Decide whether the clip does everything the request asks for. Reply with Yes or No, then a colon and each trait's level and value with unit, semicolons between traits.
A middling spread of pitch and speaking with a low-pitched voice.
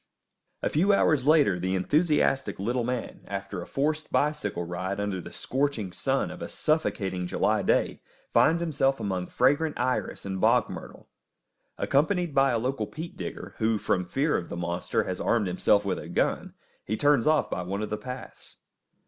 No: wide, 7.5 semitones; low, 120 Hz